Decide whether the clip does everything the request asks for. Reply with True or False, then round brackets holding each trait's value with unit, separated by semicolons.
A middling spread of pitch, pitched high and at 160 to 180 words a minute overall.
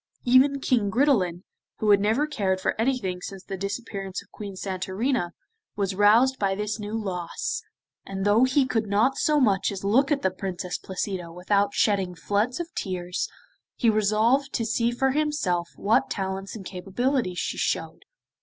True (4.5 semitones; 205 Hz; 165 wpm)